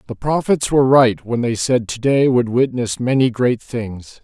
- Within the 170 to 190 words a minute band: Yes, average, 185 wpm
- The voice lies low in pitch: Yes, low, 120 Hz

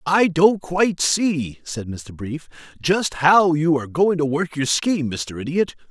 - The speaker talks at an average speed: Yes, average, 185 wpm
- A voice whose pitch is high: No, medium, 160 Hz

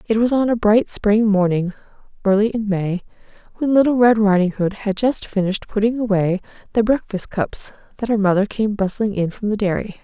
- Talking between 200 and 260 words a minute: No, average, 190 wpm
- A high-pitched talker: Yes, high, 210 Hz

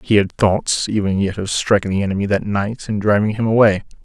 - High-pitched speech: No, low, 105 Hz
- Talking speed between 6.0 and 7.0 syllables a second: No, 5.6 syllables/s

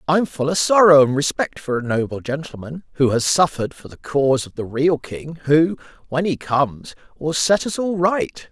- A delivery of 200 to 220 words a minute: Yes, fast, 205 wpm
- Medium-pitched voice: Yes, medium, 150 Hz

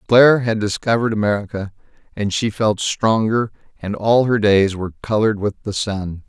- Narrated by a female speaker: No, male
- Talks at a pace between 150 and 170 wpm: Yes, average, 160 wpm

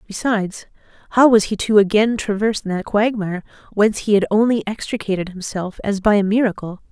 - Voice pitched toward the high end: Yes, high, 205 Hz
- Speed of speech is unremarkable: Yes, average, 165 wpm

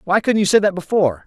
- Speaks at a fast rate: Yes, fast, 285 wpm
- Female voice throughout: No, male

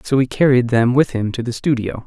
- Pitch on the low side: Yes, low, 125 Hz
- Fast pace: Yes, fast, 260 wpm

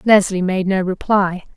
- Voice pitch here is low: No, high, 190 Hz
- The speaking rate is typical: Yes, average, 155 wpm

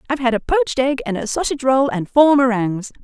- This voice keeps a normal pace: No, fast, 240 wpm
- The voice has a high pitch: Yes, very high, 255 Hz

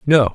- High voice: No, low, 135 Hz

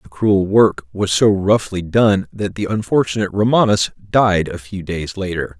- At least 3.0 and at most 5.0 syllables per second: Yes, 4.4 syllables/s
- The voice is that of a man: Yes, male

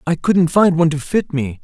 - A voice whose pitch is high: No, medium, 160 Hz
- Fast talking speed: Yes, fast, 255 wpm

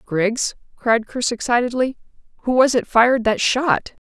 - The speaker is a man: No, female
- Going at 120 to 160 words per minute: Yes, average, 145 wpm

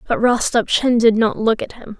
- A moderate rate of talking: No, fast, 210 wpm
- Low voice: No, high, 225 Hz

